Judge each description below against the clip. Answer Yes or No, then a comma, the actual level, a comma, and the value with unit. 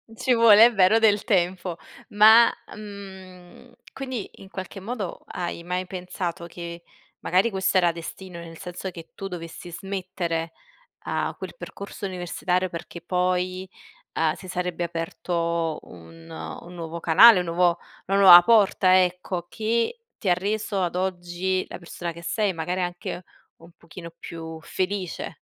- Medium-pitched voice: Yes, medium, 180 Hz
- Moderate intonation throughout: No, narrow, 2.3 semitones